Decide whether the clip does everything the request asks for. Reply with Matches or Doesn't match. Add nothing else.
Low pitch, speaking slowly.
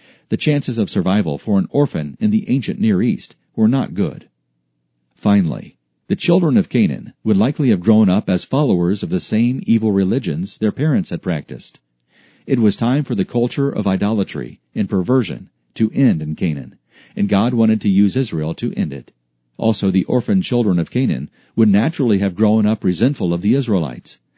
Doesn't match